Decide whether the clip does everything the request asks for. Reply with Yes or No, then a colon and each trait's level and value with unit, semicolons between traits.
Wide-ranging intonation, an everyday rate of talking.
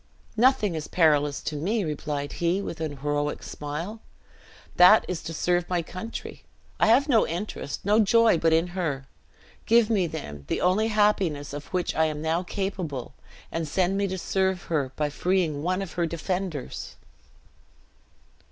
No: average, 4.4 semitones; average, 160 wpm